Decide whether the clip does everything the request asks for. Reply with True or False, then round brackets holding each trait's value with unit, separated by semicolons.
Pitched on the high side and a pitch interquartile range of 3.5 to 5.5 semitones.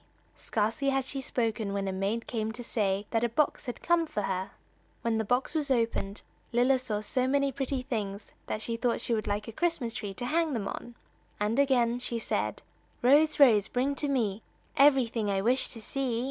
True (235 Hz; 4.0 semitones)